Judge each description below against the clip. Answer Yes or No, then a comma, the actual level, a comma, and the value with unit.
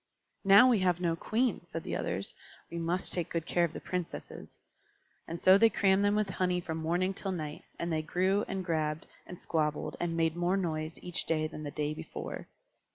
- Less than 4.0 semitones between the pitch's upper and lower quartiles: Yes, average, 2.8 semitones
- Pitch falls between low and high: Yes, medium, 175 Hz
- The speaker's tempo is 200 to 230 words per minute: Yes, fast, 205 wpm